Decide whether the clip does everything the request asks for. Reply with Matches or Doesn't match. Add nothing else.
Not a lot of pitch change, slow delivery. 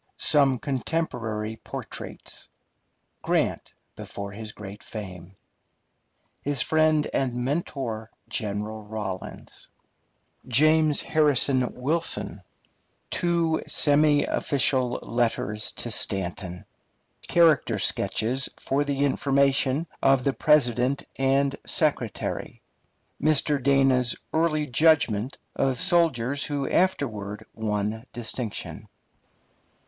Doesn't match